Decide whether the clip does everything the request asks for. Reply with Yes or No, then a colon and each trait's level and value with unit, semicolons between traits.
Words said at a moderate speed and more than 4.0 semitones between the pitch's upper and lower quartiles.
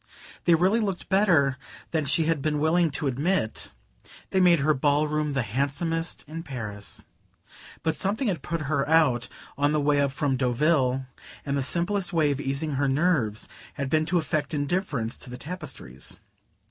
No: average, 170 wpm; average, 3.5 semitones